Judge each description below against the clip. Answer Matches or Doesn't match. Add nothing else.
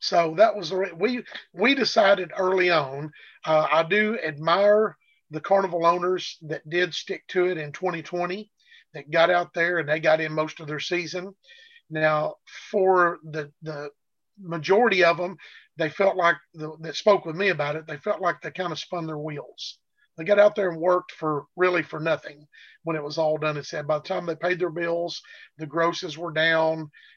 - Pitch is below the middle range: Doesn't match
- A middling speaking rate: Matches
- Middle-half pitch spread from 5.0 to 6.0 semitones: Doesn't match